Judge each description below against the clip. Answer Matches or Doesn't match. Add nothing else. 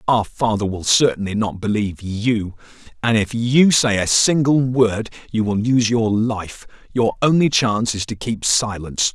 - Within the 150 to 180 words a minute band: Matches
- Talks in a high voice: Doesn't match